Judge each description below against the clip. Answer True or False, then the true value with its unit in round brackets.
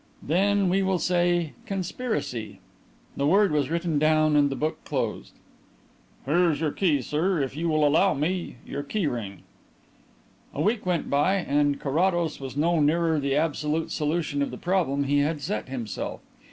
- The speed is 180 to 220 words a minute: False (170 wpm)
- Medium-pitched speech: True (155 Hz)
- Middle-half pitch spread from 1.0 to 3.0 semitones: False (3.6 semitones)